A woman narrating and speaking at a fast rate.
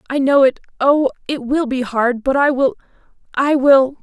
No: female; average, 150 wpm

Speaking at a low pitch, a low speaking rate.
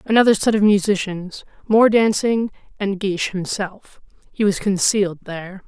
No: high, 200 Hz; slow, 125 wpm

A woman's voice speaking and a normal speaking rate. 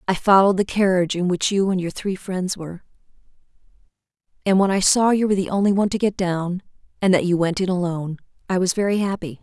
No: female; fast, 215 wpm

